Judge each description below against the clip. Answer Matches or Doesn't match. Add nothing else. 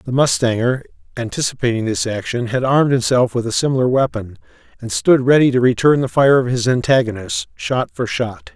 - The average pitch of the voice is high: Doesn't match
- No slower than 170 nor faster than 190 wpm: Matches